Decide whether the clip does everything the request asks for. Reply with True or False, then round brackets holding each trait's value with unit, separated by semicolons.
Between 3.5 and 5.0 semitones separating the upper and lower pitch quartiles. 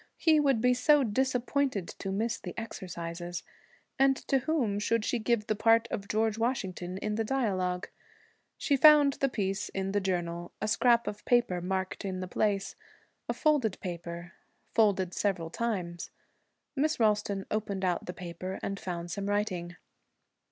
True (4.5 semitones)